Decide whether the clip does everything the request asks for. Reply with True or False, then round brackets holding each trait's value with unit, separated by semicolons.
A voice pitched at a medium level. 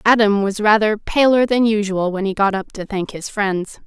False (205 Hz)